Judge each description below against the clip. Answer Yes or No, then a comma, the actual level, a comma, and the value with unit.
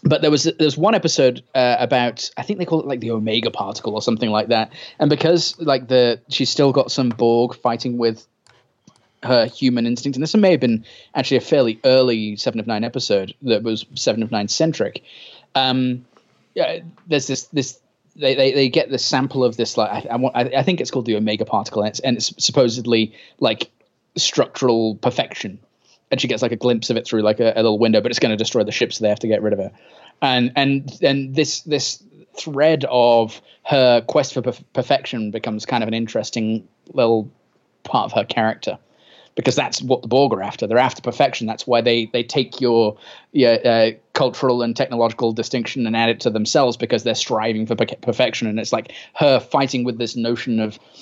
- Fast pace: Yes, fast, 215 wpm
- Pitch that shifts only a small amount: No, average, 3.1 semitones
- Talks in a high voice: No, low, 120 Hz